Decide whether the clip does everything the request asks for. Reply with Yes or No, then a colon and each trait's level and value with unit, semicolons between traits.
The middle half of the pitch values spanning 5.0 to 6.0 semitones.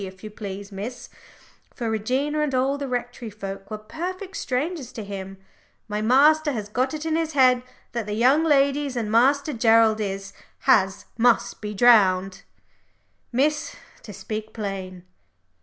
Yes: average, 5.3 semitones